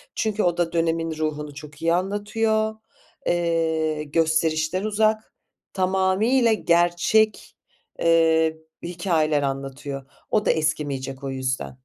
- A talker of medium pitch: Yes, medium, 165 Hz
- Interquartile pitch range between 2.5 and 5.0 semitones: Yes, average, 3.8 semitones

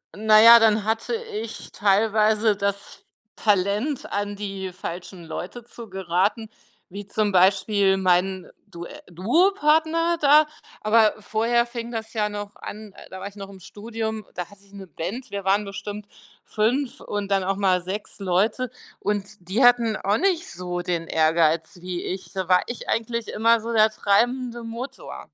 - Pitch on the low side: No, high, 205 Hz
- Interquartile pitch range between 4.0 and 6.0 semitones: No, average, 3.1 semitones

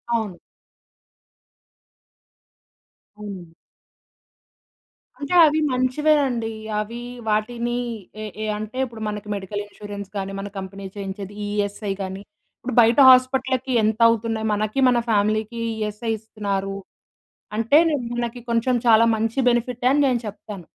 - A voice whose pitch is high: Yes, high, 220 Hz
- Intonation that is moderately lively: Yes, average, 3.0 semitones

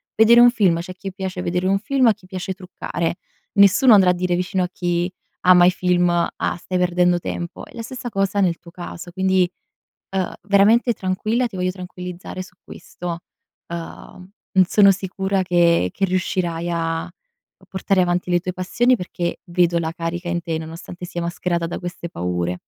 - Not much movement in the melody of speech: Yes, narrow, 1.8 semitones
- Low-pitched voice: No, medium, 180 Hz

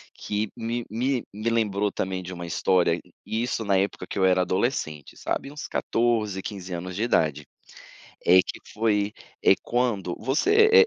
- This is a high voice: No, low, 105 Hz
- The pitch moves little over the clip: No, average, 4.2 semitones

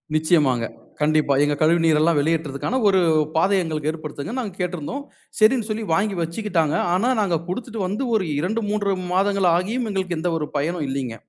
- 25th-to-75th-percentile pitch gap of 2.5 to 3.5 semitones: No, average, 4.8 semitones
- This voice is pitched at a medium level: Yes, medium, 175 Hz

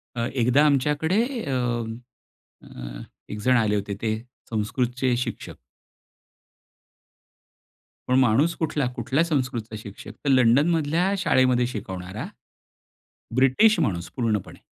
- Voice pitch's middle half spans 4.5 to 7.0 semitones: Yes, average, 5.0 semitones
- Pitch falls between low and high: No, low, 125 Hz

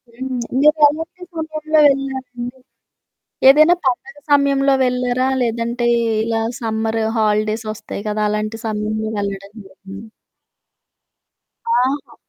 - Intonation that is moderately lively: Yes, average, 4.2 semitones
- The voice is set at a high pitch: Yes, high, 245 Hz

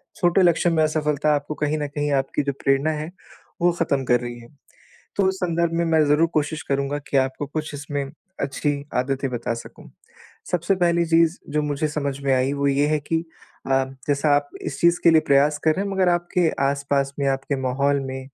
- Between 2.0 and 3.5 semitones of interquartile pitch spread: Yes, average, 3.0 semitones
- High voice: No, medium, 145 Hz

